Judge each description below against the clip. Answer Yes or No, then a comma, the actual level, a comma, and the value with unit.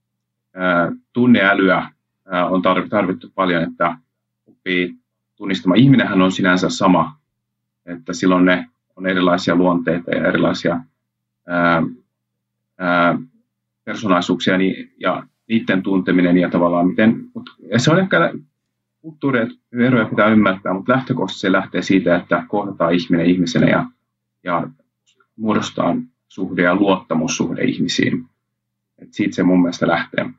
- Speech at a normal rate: Yes, average, 115 wpm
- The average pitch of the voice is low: Yes, very low, 90 Hz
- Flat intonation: Yes, narrow, 2.3 semitones